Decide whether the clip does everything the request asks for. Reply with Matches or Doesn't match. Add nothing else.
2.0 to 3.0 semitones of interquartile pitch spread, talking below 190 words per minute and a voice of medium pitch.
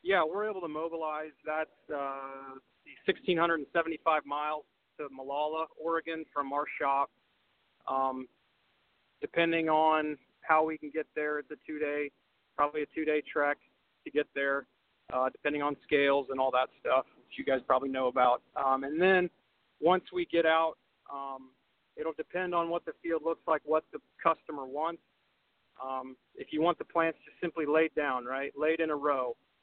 Matches